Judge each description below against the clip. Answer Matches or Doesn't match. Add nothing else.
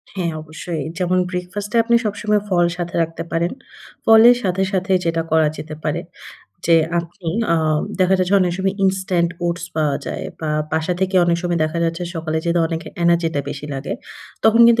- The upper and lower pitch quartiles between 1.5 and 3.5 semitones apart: Matches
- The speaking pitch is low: Doesn't match